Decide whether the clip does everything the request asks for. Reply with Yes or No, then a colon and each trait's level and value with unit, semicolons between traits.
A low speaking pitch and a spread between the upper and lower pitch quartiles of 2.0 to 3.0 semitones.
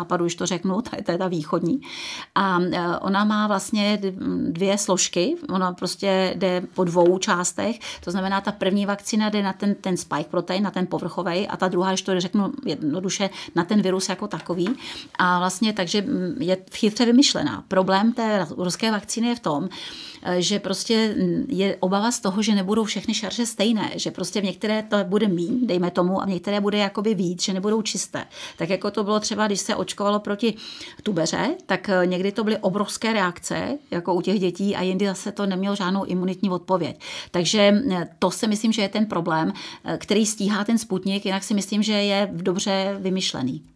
No: high, 195 Hz; narrow, 2.6 semitones